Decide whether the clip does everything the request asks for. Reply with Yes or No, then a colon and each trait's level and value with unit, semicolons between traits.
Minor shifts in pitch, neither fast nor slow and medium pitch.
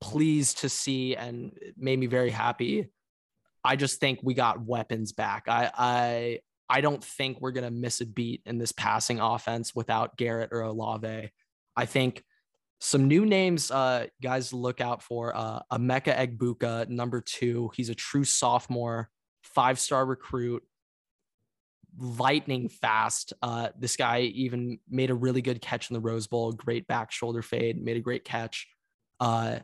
No: narrow, 1.9 semitones; average, 160 wpm; low, 120 Hz